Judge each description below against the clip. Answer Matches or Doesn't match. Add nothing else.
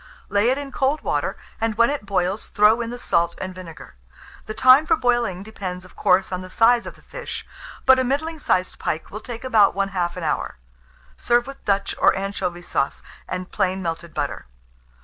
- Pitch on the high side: Matches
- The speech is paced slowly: Doesn't match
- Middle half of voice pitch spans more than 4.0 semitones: Matches